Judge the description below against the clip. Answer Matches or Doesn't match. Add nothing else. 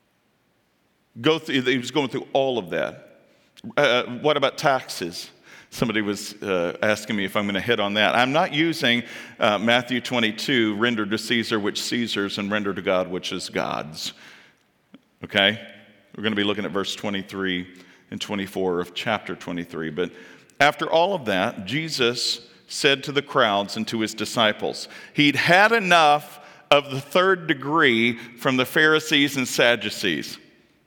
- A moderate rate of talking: Matches